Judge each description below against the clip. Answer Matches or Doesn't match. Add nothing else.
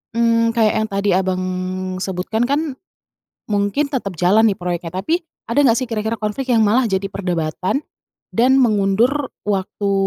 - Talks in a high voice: Matches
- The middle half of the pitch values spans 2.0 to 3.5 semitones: Doesn't match